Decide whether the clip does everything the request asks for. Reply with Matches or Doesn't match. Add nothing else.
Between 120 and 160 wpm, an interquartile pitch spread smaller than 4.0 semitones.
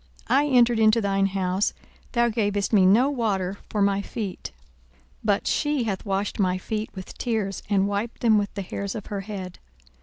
Doesn't match